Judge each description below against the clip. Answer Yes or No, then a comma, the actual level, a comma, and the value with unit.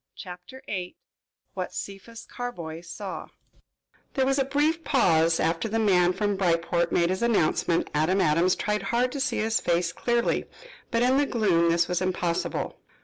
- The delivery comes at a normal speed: Yes, average, 160 wpm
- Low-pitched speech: No, high, 190 Hz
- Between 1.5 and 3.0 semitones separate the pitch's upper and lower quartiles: No, wide, 5.6 semitones